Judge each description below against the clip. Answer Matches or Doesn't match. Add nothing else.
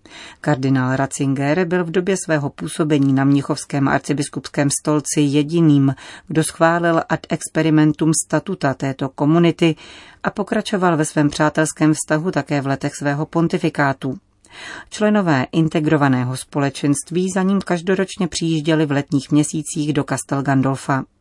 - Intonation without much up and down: Doesn't match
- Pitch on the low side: Doesn't match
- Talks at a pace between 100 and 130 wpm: Matches